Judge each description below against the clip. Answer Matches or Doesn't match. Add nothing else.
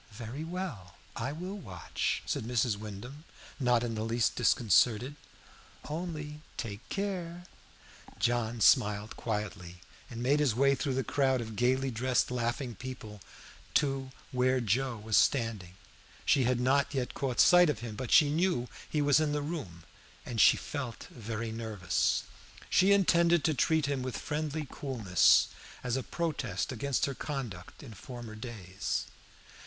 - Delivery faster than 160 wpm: Doesn't match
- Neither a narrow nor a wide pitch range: Matches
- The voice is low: Matches